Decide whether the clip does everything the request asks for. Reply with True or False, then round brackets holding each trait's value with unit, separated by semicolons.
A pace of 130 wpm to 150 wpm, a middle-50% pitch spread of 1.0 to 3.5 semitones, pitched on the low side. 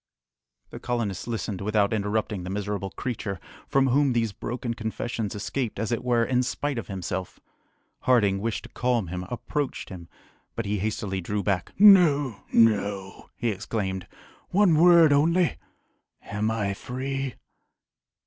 False (140 wpm; 4.3 semitones; 110 Hz)